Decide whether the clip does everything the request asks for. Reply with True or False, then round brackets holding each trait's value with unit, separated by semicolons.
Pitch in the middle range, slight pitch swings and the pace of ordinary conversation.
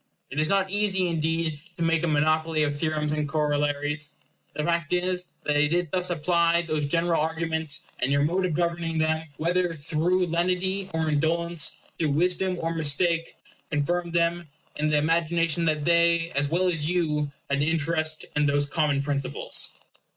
True (160 Hz; 2.3 semitones; 170 wpm)